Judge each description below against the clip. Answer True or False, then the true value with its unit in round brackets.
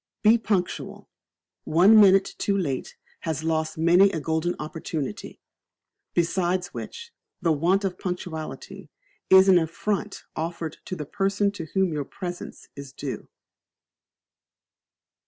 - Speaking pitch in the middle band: True (175 Hz)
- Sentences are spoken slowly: True (120 wpm)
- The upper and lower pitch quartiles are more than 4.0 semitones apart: False (3.4 semitones)